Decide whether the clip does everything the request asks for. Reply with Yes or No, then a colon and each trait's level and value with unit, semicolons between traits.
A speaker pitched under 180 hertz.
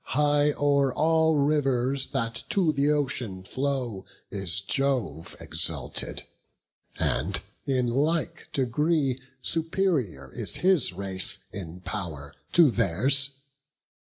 Yes: low, 135 Hz